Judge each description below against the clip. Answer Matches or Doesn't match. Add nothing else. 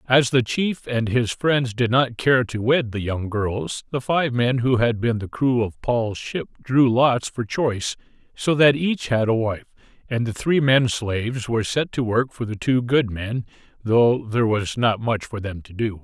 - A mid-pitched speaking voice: Doesn't match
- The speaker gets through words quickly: Matches